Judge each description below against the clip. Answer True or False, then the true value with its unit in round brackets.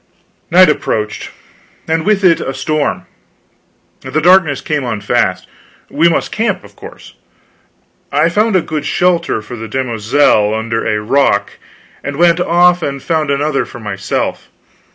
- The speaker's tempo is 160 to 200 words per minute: False (145 wpm)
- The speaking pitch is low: False (150 Hz)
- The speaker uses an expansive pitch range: True (6.7 semitones)